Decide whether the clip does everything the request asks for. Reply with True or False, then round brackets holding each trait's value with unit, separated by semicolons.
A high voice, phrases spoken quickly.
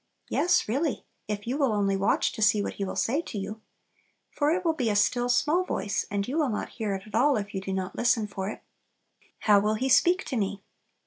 True (215 Hz; 240 wpm)